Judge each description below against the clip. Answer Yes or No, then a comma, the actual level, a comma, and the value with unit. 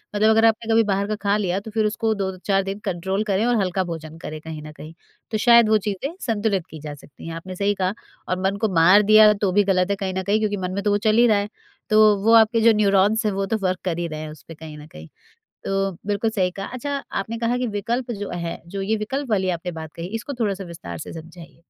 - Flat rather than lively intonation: No, average, 3.4 semitones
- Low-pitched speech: No, high, 200 Hz